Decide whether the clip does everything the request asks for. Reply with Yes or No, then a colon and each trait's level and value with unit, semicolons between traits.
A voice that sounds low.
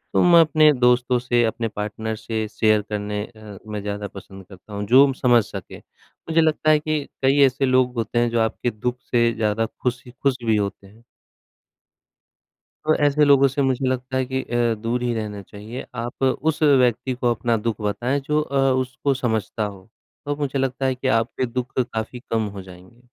Yes: low, 120 Hz